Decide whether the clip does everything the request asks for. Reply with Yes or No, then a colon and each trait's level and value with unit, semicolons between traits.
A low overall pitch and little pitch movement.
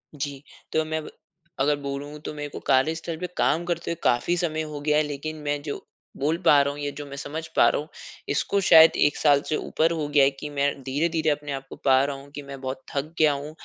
No: medium, 145 Hz; narrow, 1.9 semitones